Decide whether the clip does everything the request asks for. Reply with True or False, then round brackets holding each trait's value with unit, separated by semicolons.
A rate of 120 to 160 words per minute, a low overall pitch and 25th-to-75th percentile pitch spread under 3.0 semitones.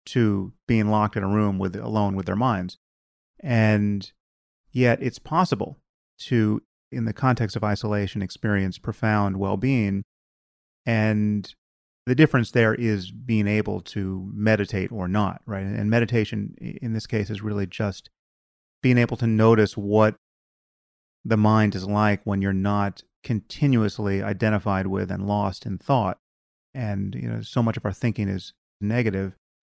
True (150 wpm; 105 Hz; 2.5 semitones)